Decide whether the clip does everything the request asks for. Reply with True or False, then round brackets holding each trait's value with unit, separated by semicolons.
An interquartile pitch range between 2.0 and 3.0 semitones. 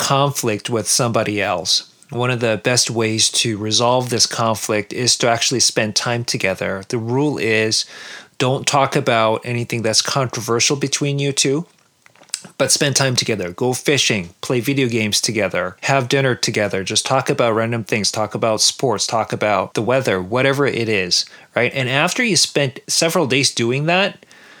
False (3.7 semitones)